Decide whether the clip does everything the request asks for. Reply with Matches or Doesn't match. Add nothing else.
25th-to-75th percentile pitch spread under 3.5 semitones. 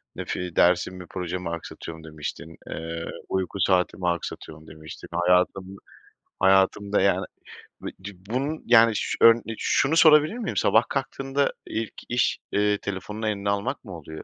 Doesn't match